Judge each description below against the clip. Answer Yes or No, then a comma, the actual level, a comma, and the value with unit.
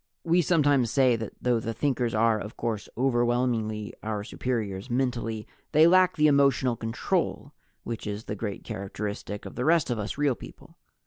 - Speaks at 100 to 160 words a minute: No, average, 170 wpm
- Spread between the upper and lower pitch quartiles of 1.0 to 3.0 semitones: No, average, 3.8 semitones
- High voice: No, low, 120 Hz